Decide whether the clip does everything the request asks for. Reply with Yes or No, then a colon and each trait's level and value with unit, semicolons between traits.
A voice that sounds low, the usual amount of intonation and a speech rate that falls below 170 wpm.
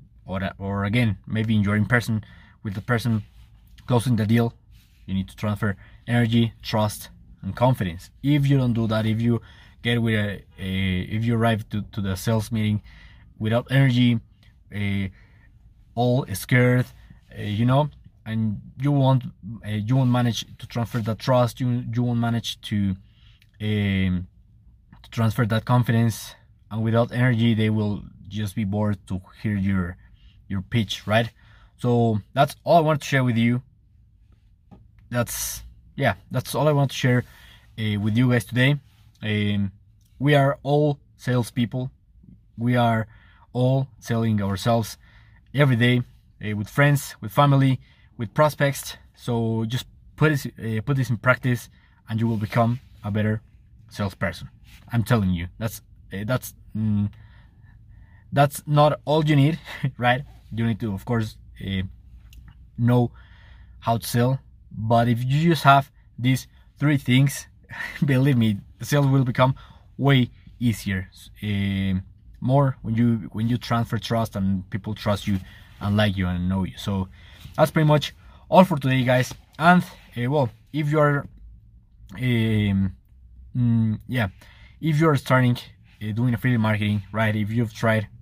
Yes: low, 110 Hz; average, 3.2 semitones; average, 155 wpm